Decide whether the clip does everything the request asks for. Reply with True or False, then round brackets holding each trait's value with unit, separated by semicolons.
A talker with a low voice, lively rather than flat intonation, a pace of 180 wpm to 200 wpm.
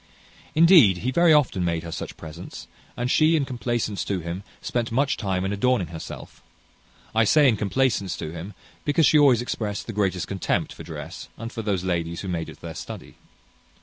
True (105 Hz; 5.9 semitones; 190 wpm)